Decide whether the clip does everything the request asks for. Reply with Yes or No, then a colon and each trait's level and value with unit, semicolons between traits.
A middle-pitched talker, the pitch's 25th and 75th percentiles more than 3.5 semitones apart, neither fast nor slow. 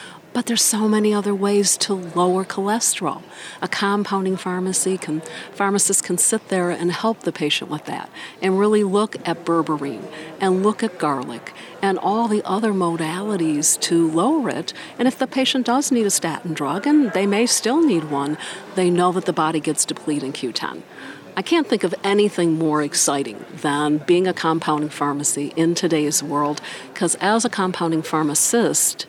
Yes: medium, 180 Hz; average, 4.7 semitones; average, 175 wpm